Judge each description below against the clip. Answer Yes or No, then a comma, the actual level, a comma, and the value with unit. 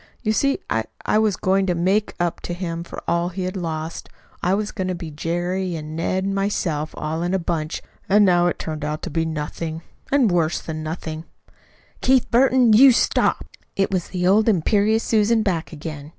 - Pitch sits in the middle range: Yes, medium, 180 Hz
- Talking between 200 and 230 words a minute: Yes, fast, 205 wpm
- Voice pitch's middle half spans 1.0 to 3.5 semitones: No, average, 4.0 semitones